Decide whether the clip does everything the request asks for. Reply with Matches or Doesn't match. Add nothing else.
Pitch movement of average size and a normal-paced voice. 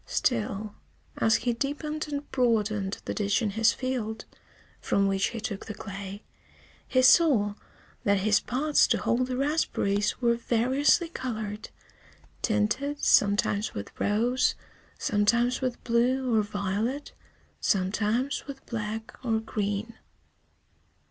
Doesn't match